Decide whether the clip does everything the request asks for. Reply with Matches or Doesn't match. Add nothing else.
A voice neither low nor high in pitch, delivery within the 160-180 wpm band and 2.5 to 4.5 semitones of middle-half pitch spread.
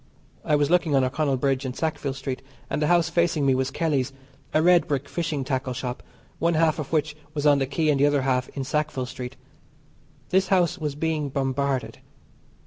Doesn't match